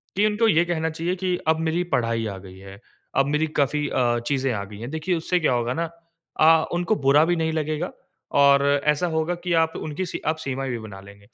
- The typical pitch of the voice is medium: Yes, medium, 155 Hz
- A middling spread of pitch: No, wide, 5.9 semitones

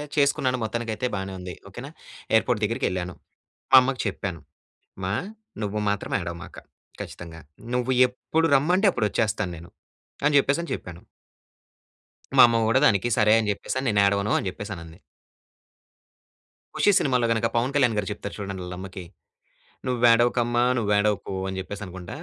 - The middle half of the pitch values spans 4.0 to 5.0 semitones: Yes, average, 4.4 semitones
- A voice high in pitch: No, low, 110 Hz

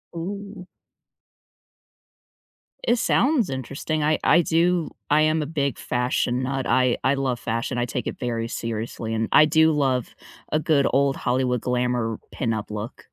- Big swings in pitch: No, average, 4.3 semitones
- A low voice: Yes, low, 130 Hz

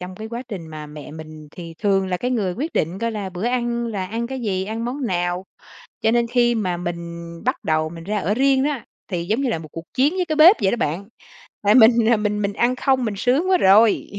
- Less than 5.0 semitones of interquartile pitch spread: No, average, 5.3 semitones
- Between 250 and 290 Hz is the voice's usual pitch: No, high, 210 Hz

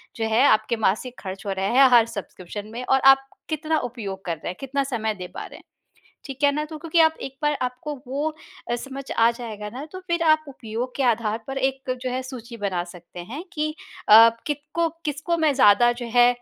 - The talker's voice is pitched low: No, very high, 250 Hz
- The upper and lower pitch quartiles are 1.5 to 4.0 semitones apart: No, average, 4.7 semitones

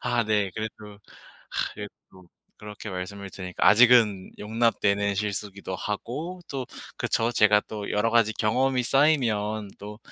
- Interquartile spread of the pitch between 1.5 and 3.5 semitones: Yes, narrow, 2.5 semitones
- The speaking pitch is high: No, low, 105 Hz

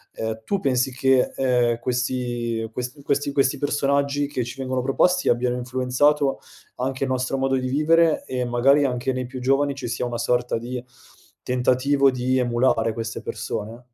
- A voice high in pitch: No, low, 130 Hz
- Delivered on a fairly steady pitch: Yes, narrow, 1.9 semitones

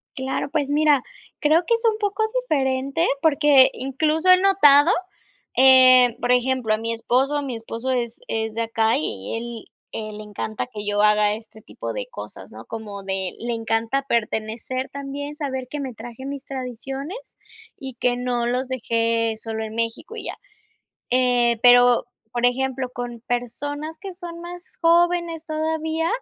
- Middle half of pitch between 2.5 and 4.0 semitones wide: No, average, 4.4 semitones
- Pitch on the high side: Yes, very high, 255 Hz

